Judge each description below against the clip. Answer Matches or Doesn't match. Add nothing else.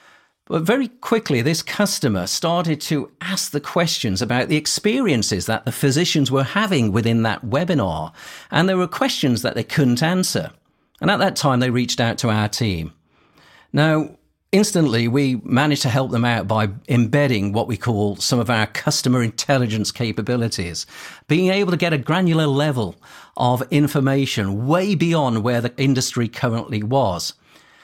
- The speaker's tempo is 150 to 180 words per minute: Matches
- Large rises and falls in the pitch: Matches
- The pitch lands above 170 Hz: Doesn't match